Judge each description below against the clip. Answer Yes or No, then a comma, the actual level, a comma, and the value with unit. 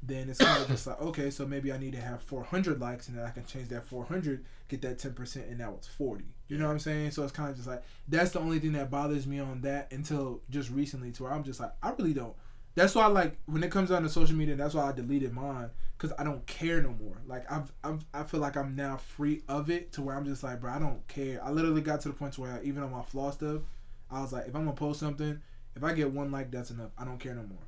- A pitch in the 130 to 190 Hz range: Yes, medium, 140 Hz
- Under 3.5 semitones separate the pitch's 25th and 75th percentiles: Yes, average, 2.9 semitones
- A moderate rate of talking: No, fast, 295 wpm